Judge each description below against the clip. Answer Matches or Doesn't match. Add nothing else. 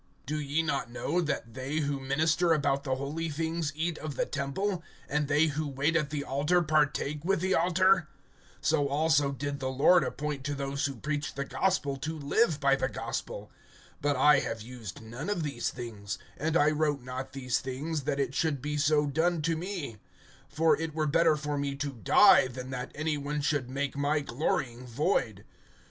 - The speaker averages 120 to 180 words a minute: Doesn't match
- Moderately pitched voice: Matches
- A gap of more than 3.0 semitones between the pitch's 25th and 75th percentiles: Doesn't match